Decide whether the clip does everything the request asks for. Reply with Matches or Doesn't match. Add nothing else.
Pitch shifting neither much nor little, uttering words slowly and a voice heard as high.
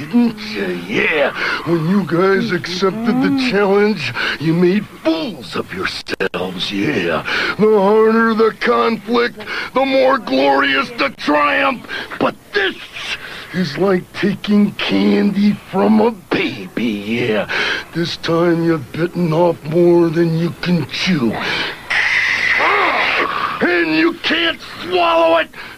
Doesn't match